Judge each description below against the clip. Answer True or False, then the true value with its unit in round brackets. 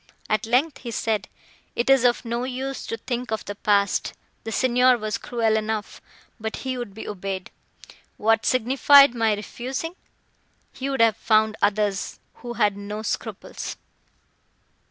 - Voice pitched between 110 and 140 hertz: False (225 Hz)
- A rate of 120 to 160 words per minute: True (150 wpm)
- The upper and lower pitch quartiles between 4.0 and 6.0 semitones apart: False (2.9 semitones)